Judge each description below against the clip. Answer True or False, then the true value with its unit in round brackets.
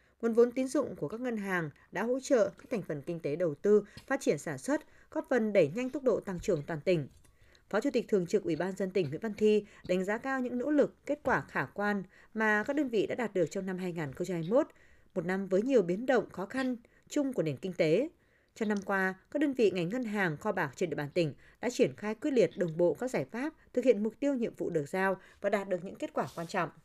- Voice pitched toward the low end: False (205 Hz)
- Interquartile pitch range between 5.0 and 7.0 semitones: True (5.5 semitones)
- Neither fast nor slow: False (265 wpm)